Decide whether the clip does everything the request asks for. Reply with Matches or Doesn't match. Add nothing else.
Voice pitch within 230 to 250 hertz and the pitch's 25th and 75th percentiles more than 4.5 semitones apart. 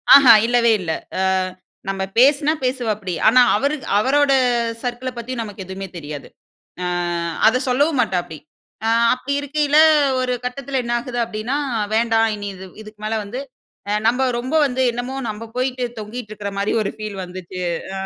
Doesn't match